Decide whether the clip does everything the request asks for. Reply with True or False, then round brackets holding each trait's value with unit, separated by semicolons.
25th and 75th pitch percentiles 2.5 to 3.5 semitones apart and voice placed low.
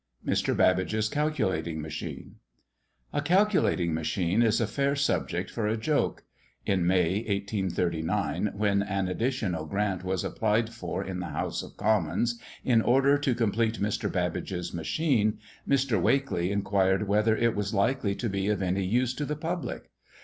False (4.2 semitones; 105 Hz)